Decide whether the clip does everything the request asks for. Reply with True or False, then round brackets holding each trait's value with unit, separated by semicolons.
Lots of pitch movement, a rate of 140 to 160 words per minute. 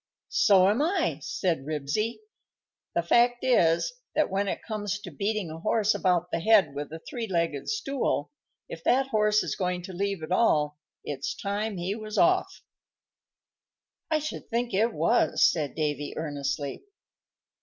True (5.7 semitones; 155 wpm)